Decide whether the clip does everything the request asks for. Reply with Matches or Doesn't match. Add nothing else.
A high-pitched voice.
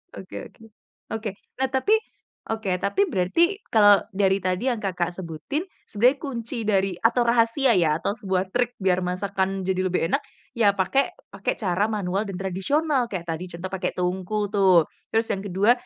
Matches